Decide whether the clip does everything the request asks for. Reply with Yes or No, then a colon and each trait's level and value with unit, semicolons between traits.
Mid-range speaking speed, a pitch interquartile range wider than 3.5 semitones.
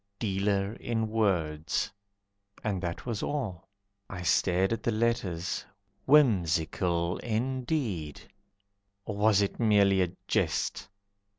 No: slow, 105 wpm; average, 4.2 semitones